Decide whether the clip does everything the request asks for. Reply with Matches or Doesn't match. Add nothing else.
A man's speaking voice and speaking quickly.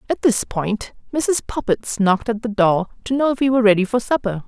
Doesn't match